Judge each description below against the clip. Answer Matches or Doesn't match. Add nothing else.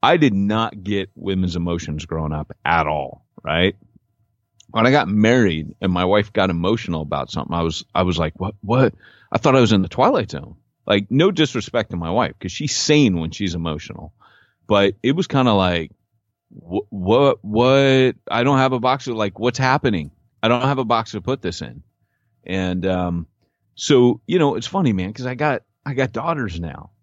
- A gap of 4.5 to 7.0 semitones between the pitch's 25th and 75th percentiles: Matches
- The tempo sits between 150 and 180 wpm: Doesn't match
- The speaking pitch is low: Matches